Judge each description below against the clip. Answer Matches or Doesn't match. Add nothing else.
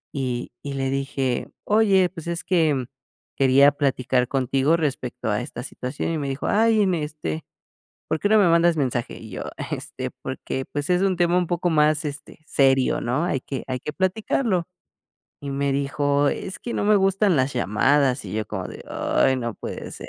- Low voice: Doesn't match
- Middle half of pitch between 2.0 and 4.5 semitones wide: Doesn't match